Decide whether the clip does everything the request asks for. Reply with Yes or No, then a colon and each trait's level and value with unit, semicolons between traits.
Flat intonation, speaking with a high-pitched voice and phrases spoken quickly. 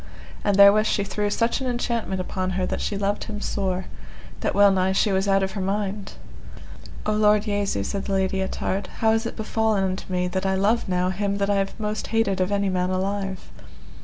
Yes: narrow, 1.8 semitones; high, 200 Hz; fast, 215 wpm